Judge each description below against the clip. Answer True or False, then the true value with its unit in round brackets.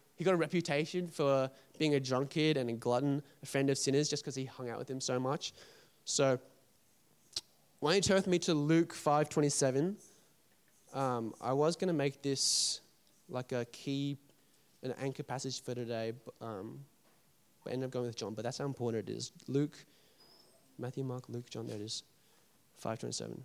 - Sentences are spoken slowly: False (190 wpm)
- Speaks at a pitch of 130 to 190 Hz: True (135 Hz)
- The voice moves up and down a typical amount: True (3.1 semitones)